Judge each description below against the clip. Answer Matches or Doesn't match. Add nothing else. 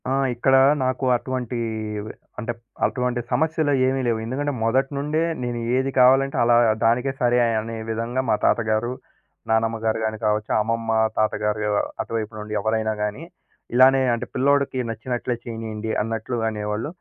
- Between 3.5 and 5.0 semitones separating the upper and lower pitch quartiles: Doesn't match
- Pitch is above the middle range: Doesn't match